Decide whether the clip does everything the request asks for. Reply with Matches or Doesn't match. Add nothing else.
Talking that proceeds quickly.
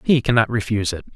Matches